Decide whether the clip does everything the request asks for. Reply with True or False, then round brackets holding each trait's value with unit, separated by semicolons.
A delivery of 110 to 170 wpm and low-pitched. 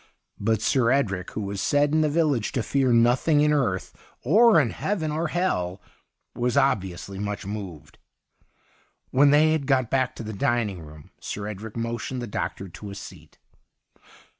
True (165 wpm; 120 Hz)